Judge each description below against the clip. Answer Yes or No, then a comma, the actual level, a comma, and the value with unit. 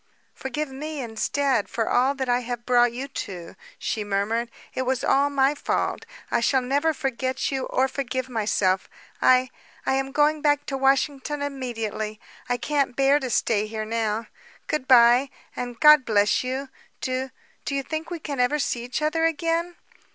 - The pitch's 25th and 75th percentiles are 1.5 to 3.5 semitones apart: Yes, average, 3.1 semitones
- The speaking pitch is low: No, very high, 260 Hz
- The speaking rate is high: No, average, 175 wpm